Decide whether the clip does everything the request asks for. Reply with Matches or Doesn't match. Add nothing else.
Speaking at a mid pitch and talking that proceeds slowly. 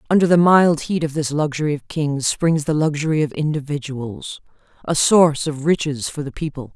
Doesn't match